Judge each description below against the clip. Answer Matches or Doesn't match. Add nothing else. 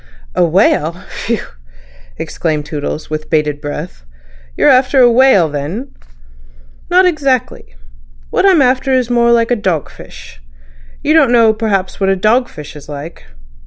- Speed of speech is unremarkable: Matches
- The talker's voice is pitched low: Doesn't match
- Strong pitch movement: Matches